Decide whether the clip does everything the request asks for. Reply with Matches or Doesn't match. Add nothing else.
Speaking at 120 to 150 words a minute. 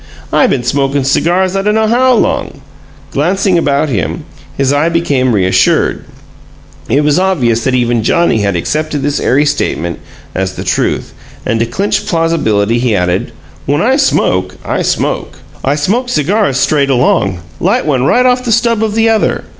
Doesn't match